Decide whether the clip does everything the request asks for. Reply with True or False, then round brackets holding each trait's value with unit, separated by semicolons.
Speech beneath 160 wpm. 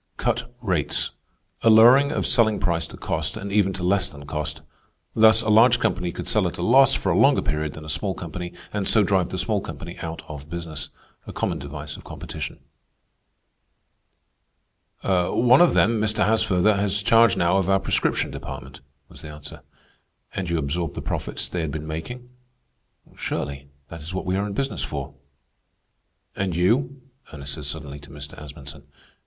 False (175 wpm)